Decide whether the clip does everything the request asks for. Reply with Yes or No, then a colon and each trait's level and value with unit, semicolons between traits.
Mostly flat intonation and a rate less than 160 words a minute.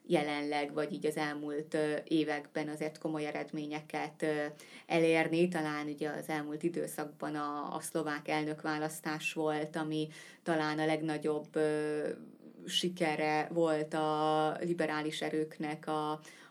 Yes: narrow, 0.8 semitones; average, 110 wpm